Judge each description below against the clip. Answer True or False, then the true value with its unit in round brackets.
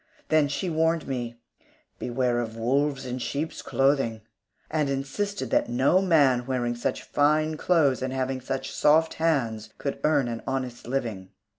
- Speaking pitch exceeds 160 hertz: False (135 Hz)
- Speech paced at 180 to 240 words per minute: False (150 wpm)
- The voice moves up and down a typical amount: True (3.9 semitones)